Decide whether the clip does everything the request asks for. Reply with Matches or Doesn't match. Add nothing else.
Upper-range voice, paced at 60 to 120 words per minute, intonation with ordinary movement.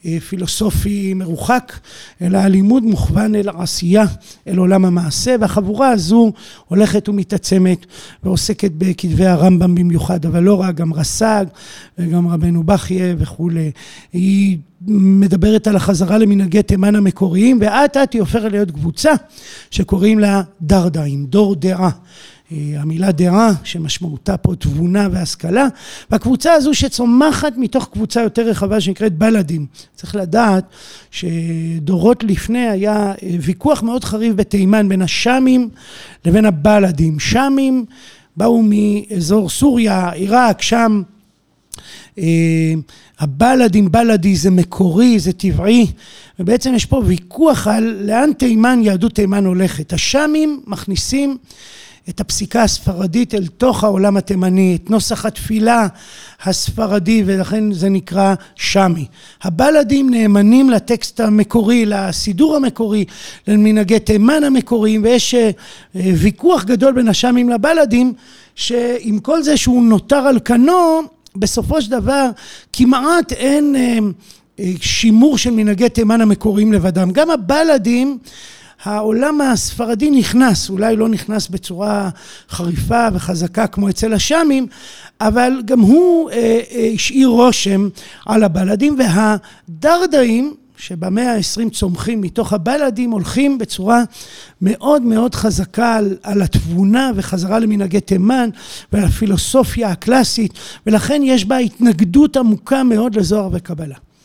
Matches